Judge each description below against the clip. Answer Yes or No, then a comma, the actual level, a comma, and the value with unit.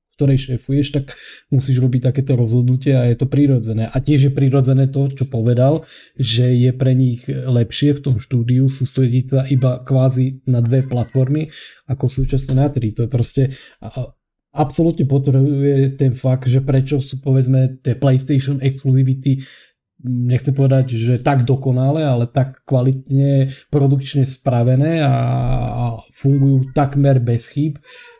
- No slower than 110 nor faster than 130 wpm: No, average, 140 wpm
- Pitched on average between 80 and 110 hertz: No, low, 130 Hz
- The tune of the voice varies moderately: No, narrow, 1.4 semitones